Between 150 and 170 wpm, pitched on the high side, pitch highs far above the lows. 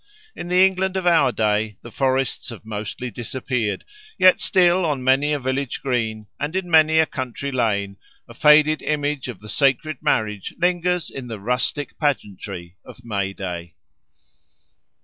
No: average, 155 wpm; low, 130 Hz; wide, 6.0 semitones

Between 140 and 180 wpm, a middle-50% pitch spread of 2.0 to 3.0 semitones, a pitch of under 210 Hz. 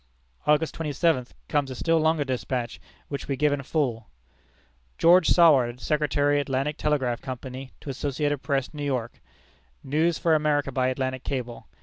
Yes: average, 150 wpm; average, 2.7 semitones; medium, 140 Hz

